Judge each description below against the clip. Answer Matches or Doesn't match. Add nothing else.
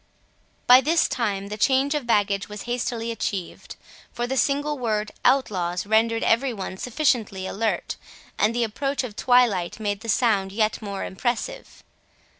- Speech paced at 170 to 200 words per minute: Doesn't match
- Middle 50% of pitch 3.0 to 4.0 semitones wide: Matches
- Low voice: Doesn't match